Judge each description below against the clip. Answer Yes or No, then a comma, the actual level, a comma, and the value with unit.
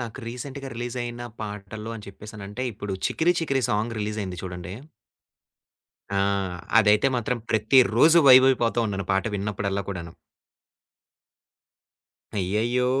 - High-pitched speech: No, low, 110 Hz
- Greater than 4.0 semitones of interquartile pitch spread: No, average, 3.6 semitones